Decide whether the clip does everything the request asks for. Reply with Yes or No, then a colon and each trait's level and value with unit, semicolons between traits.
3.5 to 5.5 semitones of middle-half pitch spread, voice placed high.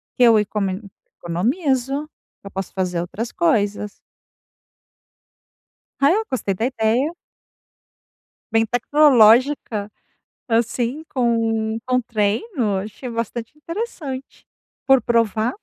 Yes: average, 4.0 semitones; high, 230 Hz